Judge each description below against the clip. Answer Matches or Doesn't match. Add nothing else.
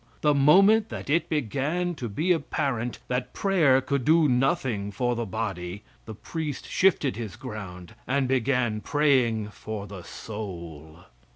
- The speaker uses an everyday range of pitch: Doesn't match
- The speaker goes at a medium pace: Matches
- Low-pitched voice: Matches